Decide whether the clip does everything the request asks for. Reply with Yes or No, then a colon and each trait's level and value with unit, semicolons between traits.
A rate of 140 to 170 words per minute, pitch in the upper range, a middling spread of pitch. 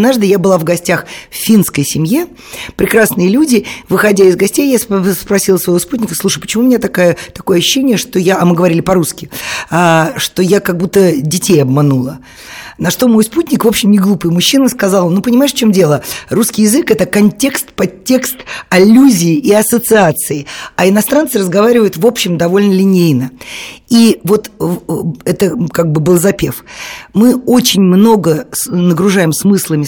Yes: fast, 160 wpm; high, 195 Hz; average, 4.0 semitones